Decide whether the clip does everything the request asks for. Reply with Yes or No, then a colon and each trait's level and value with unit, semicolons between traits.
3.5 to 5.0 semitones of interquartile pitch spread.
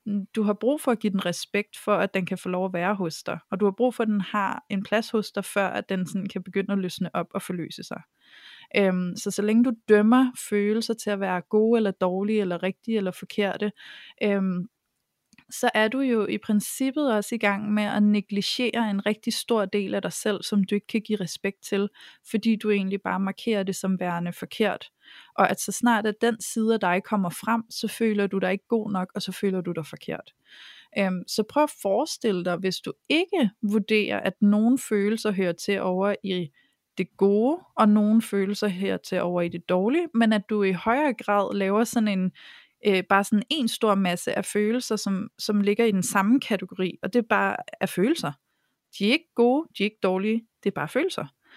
No: narrow, 2.6 semitones